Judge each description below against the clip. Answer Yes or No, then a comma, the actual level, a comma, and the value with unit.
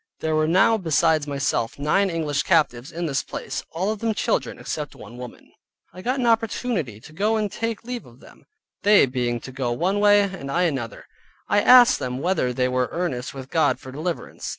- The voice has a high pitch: No, medium, 160 Hz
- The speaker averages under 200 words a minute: No, fast, 205 wpm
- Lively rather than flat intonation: Yes, wide, 7.7 semitones